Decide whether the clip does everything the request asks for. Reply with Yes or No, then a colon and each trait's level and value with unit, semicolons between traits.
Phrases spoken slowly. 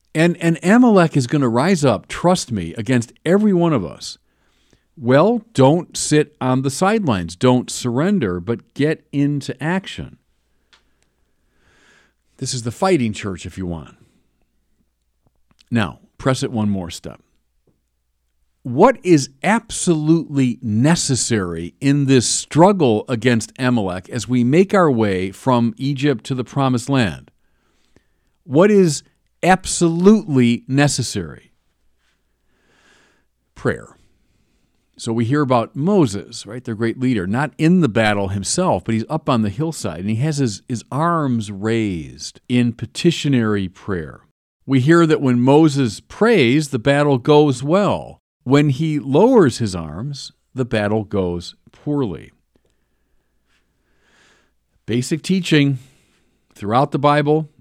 Yes: slow, 125 wpm